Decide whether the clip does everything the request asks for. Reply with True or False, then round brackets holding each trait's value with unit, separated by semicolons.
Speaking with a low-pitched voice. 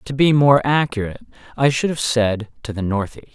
True (125 Hz)